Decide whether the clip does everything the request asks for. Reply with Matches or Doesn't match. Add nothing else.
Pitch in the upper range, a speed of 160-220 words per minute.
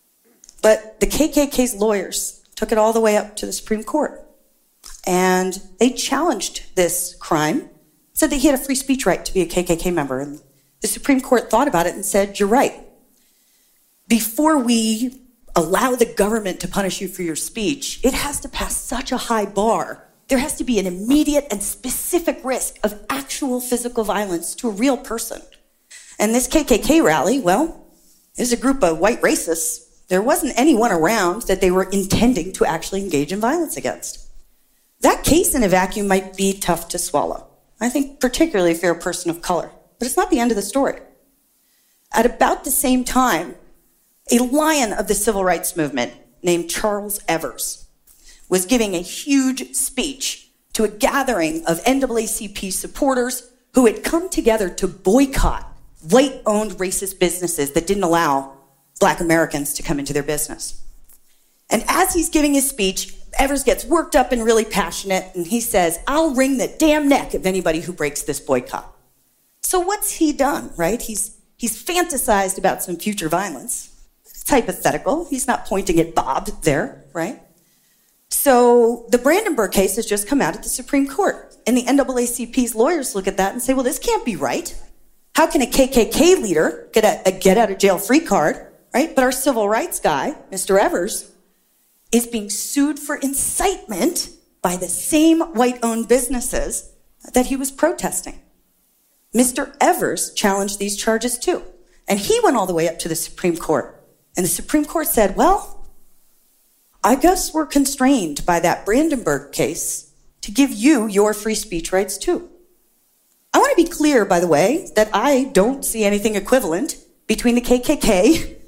Matches